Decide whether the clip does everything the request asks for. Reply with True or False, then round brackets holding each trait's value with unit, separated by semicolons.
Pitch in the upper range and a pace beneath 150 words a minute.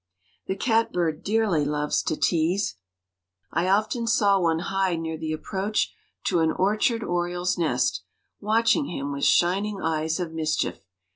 False (175 Hz; 140 wpm)